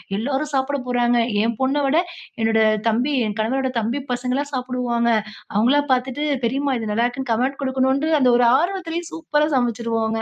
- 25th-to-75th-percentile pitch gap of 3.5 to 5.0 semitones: No, average, 3.1 semitones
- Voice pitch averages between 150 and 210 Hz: No, very high, 255 Hz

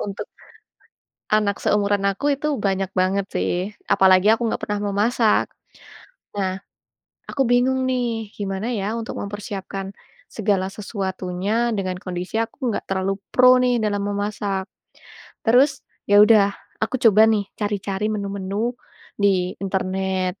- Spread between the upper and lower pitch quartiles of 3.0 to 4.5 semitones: No, narrow, 2.6 semitones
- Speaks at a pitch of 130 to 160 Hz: No, high, 205 Hz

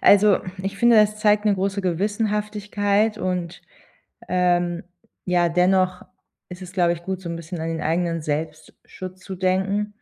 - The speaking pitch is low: No, medium, 185 Hz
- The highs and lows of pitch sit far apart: No, average, 2.8 semitones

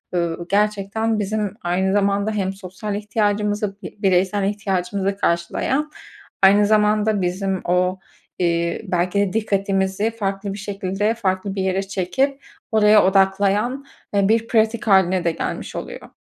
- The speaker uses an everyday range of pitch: No, narrow, 1.8 semitones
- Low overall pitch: No, high, 200 Hz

